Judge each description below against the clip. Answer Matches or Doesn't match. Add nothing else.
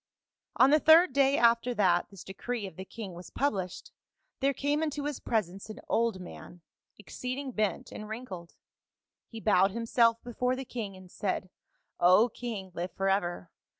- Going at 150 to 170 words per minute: Matches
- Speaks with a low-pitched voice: Doesn't match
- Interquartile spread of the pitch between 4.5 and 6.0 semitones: Matches